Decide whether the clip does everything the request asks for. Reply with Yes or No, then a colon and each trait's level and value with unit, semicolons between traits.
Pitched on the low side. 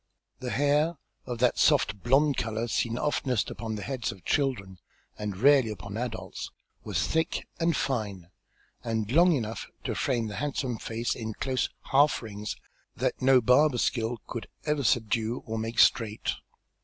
Yes: low, 120 Hz